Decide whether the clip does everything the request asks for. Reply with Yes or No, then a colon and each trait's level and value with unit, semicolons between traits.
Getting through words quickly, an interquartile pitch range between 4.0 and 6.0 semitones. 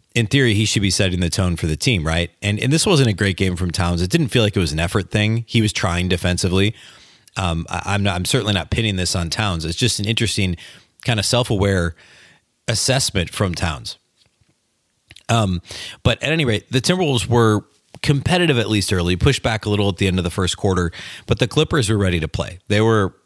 Yes: fast, 225 wpm; average, 4.5 semitones